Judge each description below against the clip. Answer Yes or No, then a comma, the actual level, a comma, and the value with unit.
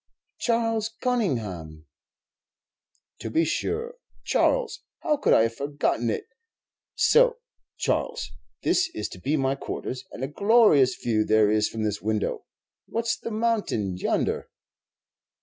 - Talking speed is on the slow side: Yes, slow, 130 wpm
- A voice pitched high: No, medium, 145 Hz